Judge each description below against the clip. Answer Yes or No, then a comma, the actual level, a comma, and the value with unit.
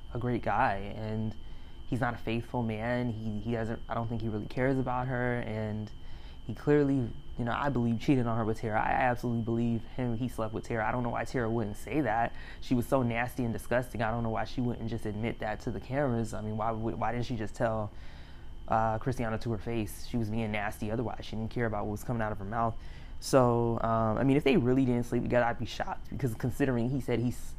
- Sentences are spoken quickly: Yes, fast, 245 wpm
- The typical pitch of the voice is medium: No, low, 115 Hz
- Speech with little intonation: Yes, narrow, 2.0 semitones